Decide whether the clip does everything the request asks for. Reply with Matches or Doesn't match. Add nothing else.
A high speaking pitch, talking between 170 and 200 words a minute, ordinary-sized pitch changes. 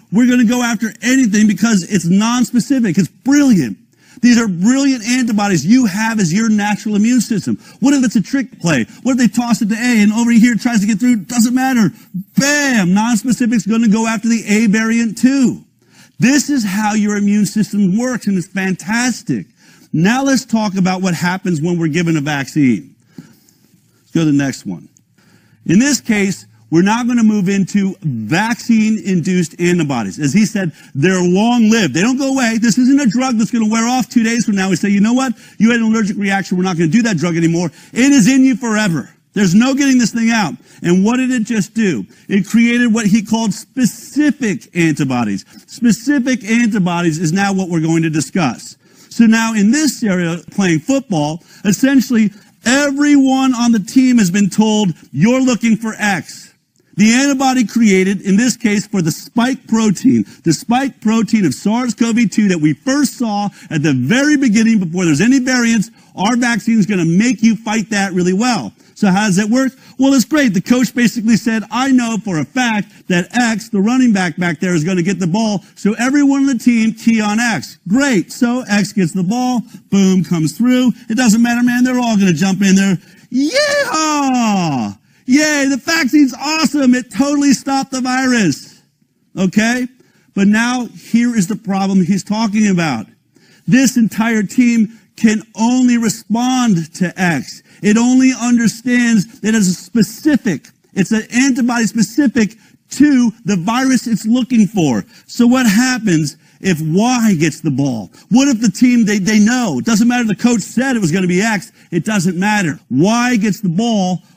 Matches